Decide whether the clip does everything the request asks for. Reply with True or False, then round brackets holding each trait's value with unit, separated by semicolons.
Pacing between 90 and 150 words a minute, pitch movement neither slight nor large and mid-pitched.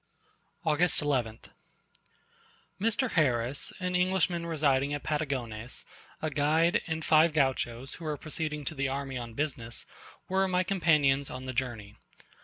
True (135 wpm; 3.9 semitones; 145 Hz)